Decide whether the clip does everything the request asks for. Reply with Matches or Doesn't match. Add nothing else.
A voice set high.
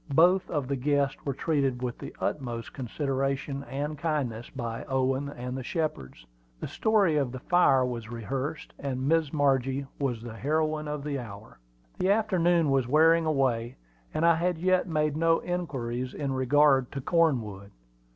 Doesn't match